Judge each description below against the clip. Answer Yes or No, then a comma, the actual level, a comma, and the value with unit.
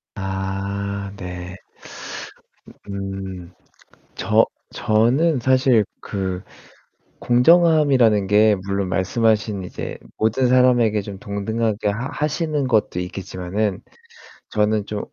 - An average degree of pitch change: Yes, average, 3.9 semitones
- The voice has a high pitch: No, low, 105 Hz